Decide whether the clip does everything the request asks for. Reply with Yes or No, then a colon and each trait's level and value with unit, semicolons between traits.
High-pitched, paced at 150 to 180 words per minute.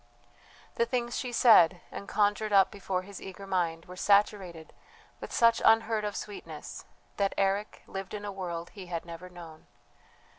Yes: high, 195 Hz; average, 160 wpm